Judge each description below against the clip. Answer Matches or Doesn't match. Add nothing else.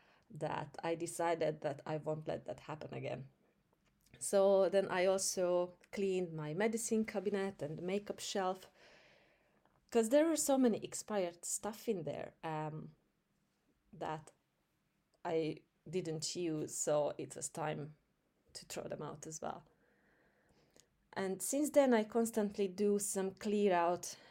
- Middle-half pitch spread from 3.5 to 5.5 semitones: Matches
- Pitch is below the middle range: Doesn't match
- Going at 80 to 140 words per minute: Matches